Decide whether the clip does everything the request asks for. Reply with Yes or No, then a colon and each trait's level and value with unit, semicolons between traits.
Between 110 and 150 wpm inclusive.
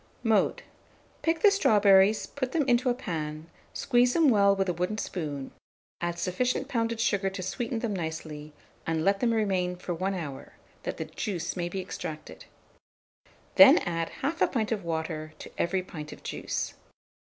No: average, 165 wpm